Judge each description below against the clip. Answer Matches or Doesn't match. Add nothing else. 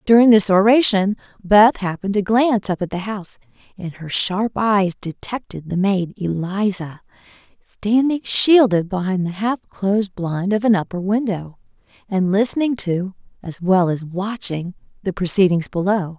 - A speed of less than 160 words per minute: Matches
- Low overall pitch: Doesn't match